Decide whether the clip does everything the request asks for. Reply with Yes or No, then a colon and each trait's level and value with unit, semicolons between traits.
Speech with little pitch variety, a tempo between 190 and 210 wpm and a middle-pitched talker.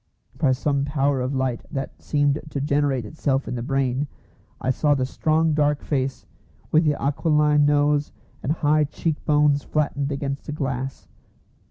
No: narrow, 1.6 semitones; average, 160 wpm; medium, 145 Hz